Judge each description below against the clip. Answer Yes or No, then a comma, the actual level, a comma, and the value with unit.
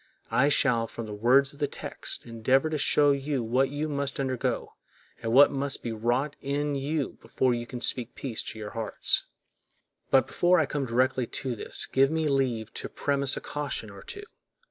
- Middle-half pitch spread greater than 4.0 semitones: No, average, 3.2 semitones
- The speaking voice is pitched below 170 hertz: Yes, low, 135 Hz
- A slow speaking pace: No, average, 190 wpm